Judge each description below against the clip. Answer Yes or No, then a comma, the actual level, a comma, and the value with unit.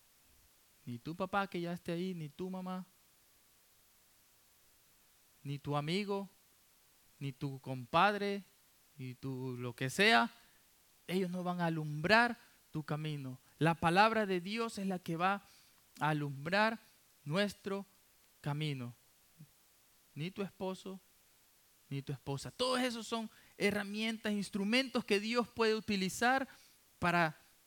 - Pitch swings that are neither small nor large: No, wide, 5.9 semitones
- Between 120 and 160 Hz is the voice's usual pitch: No, medium, 180 Hz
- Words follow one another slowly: Yes, slow, 120 wpm